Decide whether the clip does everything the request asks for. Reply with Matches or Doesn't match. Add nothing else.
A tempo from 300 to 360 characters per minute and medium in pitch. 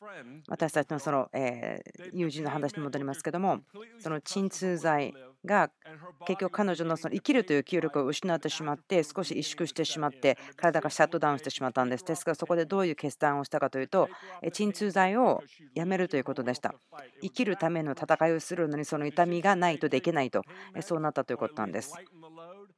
Doesn't match